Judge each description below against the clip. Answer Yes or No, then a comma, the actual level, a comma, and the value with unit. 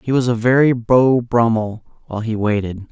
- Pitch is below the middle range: Yes, low, 115 Hz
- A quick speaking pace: No, average, 185 wpm